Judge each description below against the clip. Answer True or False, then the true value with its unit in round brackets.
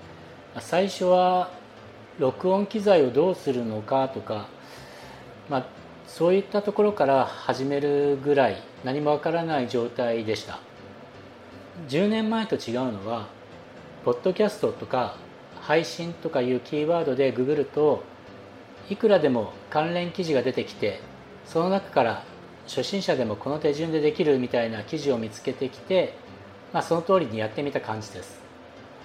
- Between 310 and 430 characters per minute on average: False (285 characters per minute)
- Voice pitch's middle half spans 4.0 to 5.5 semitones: False (7.5 semitones)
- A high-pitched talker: False (145 Hz)